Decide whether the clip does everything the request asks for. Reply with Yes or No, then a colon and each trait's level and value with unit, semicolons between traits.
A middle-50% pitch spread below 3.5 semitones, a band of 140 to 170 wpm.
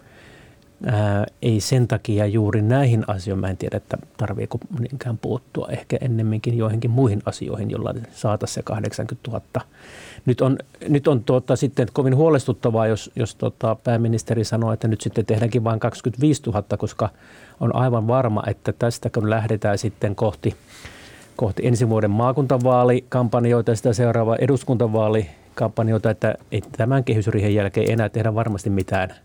Yes: narrow, 2.6 semitones; average, 145 wpm